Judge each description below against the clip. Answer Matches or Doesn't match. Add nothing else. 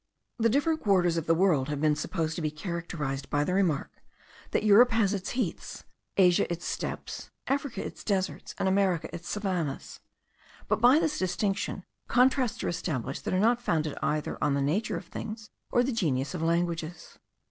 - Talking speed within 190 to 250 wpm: Doesn't match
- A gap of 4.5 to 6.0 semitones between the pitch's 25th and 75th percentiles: Matches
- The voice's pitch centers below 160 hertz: Doesn't match